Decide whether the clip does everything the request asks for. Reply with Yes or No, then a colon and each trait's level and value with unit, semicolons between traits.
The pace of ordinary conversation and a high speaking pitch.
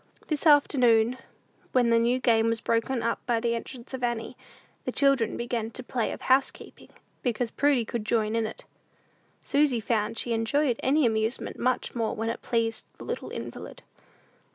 Yes: average, 170 wpm; high, 235 Hz